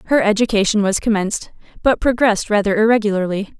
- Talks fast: No, slow, 135 wpm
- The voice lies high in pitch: Yes, high, 210 Hz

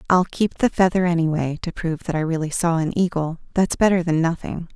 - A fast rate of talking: Yes, fast, 215 wpm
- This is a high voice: No, medium, 170 Hz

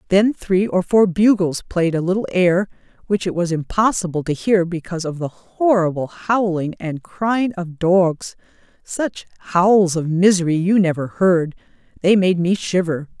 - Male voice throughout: No, female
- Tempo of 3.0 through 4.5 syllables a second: Yes, 4.4 syllables/s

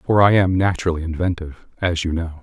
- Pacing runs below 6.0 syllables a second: No, 6.2 syllables/s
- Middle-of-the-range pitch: No, very low, 85 Hz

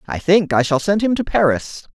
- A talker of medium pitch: Yes, medium, 175 Hz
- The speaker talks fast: Yes, fast, 245 wpm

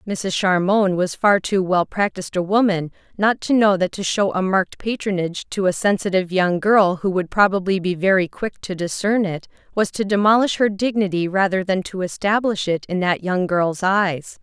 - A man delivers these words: No, female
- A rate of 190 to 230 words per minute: Yes, average, 195 wpm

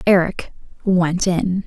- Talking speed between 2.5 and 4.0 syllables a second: Yes, 3.3 syllables/s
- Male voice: No, female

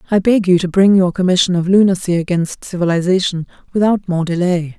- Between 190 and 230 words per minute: No, average, 175 wpm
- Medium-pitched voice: Yes, medium, 180 Hz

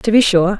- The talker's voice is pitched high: Yes, high, 200 Hz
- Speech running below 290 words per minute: No, fast, 300 wpm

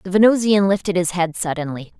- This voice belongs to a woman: Yes, female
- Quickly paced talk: No, average, 180 wpm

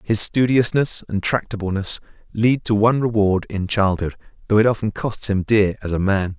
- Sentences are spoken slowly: No, average, 180 wpm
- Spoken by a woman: No, male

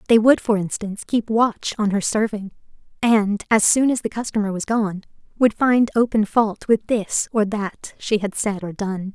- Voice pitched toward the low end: No, high, 215 Hz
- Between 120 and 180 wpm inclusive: No, average, 195 wpm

